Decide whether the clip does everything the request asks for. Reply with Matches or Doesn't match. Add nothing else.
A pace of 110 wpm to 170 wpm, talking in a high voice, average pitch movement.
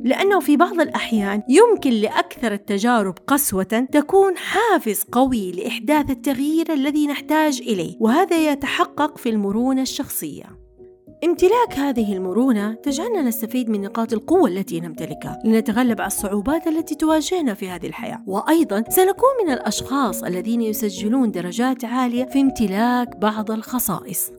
Doesn't match